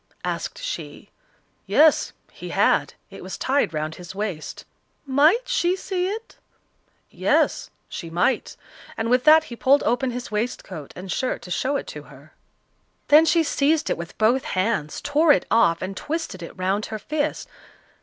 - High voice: Yes, very high, 250 Hz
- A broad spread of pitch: Yes, wide, 8.6 semitones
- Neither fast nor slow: Yes, average, 165 wpm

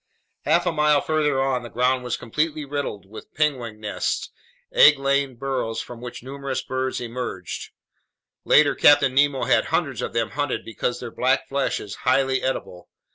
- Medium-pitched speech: No, low, 130 Hz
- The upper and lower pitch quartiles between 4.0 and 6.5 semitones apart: No, average, 2.9 semitones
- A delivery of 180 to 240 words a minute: No, average, 165 wpm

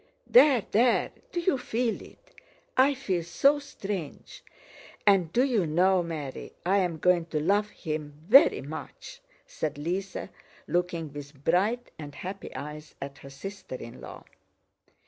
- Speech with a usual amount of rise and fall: No, wide, 5.8 semitones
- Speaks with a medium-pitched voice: Yes, medium, 180 Hz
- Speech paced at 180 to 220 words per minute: No, average, 145 wpm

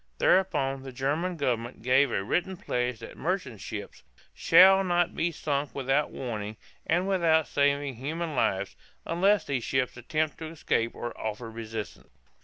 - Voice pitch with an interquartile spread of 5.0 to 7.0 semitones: Yes, wide, 5.6 semitones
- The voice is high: No, medium, 140 Hz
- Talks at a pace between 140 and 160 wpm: Yes, average, 150 wpm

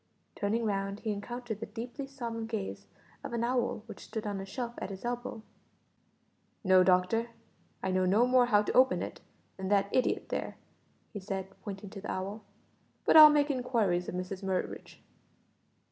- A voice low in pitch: No, high, 215 Hz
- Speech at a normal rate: Yes, average, 175 wpm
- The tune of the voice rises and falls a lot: No, average, 3.9 semitones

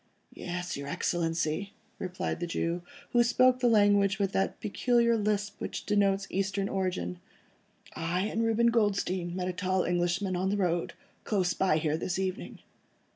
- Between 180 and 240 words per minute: No, average, 155 wpm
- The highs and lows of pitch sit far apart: No, average, 2.7 semitones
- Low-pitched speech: No, high, 190 Hz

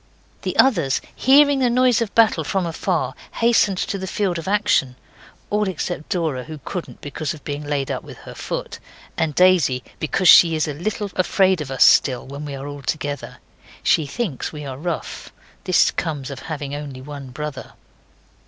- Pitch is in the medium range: Yes, medium, 155 Hz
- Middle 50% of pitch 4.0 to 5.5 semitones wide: Yes, average, 5.2 semitones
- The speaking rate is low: No, average, 180 wpm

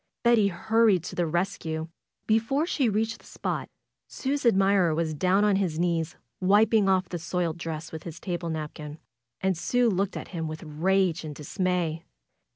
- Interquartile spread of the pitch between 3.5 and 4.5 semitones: Yes, average, 4.0 semitones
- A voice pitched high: No, medium, 180 Hz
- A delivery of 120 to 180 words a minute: Yes, average, 165 wpm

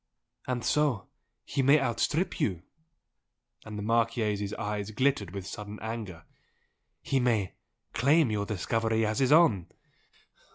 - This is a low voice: Yes, low, 110 Hz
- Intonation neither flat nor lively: Yes, average, 4.0 semitones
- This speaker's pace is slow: Yes, slow, 125 wpm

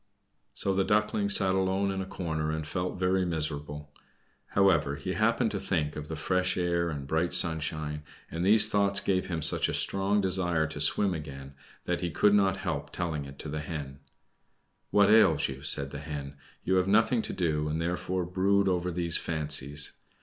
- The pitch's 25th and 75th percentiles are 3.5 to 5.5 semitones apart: Yes, average, 4.0 semitones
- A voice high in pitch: No, very low, 85 Hz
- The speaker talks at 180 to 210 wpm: Yes, average, 185 wpm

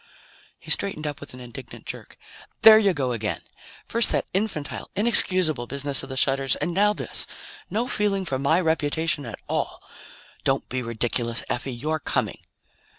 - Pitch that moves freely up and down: Yes, wide, 6.4 semitones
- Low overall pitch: No, medium, 145 Hz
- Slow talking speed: No, average, 160 wpm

